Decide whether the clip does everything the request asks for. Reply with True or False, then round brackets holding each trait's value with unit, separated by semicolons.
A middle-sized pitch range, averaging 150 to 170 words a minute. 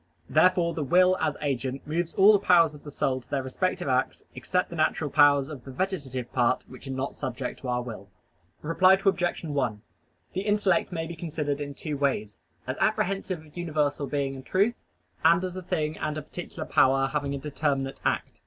False (4.6 semitones; 200 wpm)